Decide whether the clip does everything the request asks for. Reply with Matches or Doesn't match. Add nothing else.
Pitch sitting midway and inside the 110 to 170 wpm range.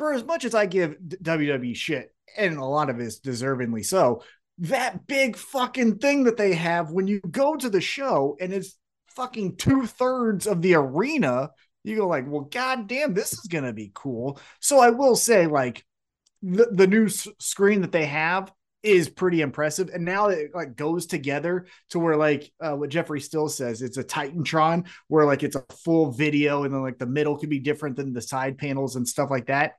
Doesn't match